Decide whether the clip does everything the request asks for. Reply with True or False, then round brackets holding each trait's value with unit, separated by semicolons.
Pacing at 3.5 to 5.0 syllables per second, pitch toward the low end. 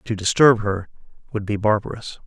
False (5.4 syllables/s; 110 Hz)